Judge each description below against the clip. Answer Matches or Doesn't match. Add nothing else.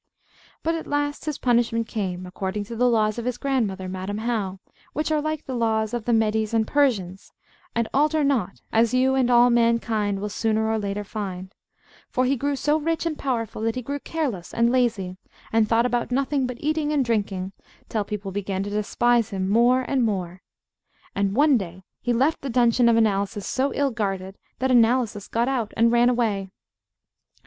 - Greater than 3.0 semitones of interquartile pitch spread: Matches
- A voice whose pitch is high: Matches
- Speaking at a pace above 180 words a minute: Matches